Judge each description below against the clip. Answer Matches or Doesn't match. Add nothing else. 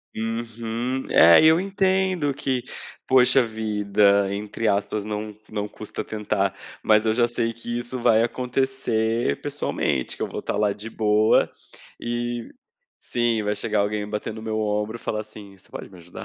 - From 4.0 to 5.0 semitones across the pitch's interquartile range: Doesn't match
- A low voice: Matches